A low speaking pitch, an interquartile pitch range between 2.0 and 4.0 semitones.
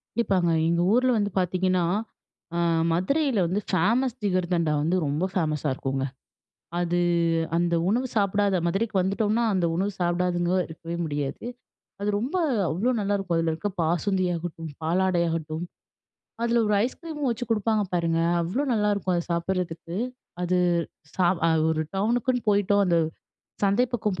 No: medium, 185 Hz; average, 3.6 semitones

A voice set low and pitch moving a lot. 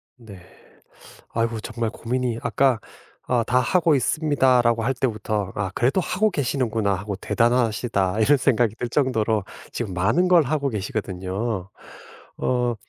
No: low, 120 Hz; average, 3.6 semitones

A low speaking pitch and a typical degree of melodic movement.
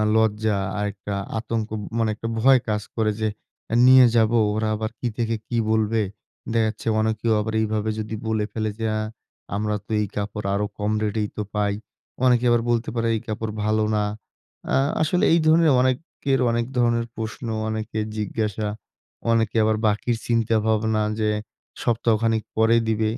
No: low, 110 Hz; narrow, 1.4 semitones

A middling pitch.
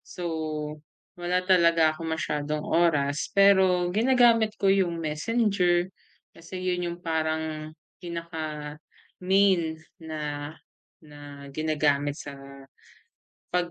Yes: medium, 170 Hz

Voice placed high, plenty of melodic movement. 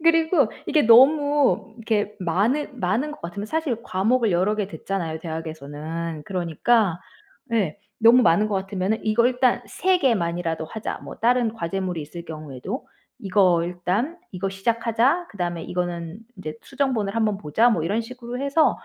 Yes: high, 205 Hz; wide, 5.8 semitones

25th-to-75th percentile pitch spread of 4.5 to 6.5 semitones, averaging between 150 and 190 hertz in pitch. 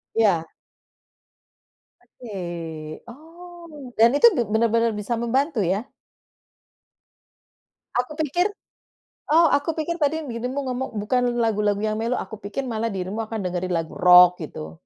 No: wide, 5.5 semitones; high, 230 Hz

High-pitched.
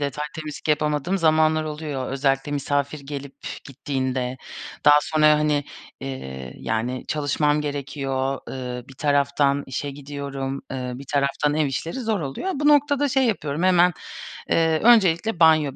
No: medium, 145 Hz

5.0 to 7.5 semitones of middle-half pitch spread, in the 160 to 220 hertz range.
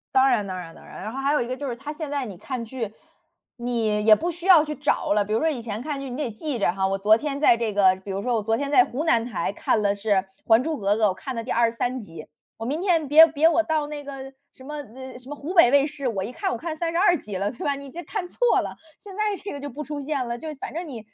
No: average, 5.3 semitones; very high, 265 Hz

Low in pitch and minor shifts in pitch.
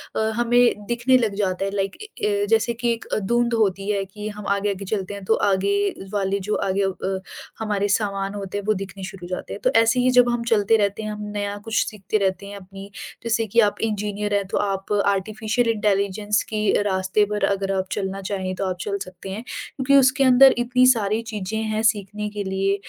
No: high, 205 Hz; narrow, 2.2 semitones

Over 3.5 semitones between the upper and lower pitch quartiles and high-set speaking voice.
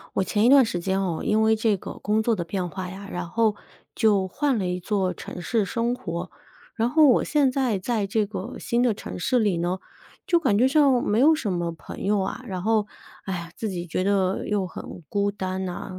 Yes: average, 3.9 semitones; high, 205 Hz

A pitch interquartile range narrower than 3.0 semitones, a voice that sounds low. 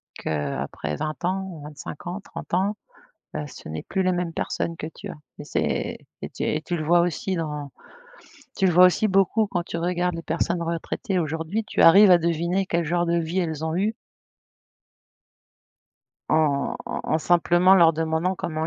No: narrow, 2.5 semitones; medium, 170 Hz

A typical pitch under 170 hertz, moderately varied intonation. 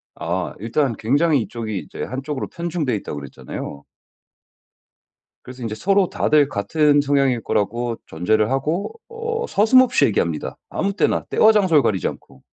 No: low, 135 Hz; wide, 7.7 semitones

